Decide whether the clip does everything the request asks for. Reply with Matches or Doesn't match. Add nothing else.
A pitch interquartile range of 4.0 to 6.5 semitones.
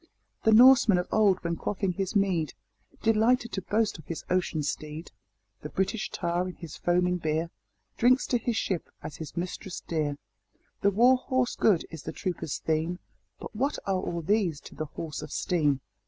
Matches